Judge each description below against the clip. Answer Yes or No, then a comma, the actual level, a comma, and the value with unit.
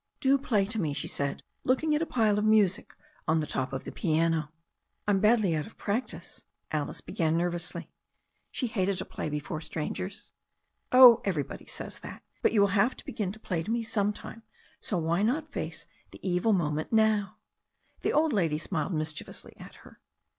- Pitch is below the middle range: No, high, 195 Hz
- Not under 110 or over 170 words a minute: No, average, 185 wpm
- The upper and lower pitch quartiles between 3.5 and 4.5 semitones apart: No, wide, 5.4 semitones